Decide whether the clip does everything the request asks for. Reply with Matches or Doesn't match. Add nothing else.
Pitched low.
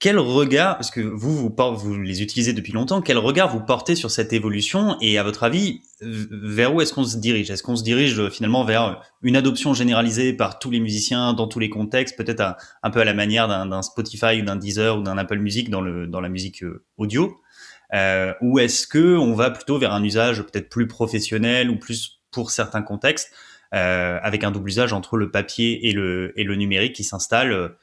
Matches